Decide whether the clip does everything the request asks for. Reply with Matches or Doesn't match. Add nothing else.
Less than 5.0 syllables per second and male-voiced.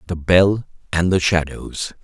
Matches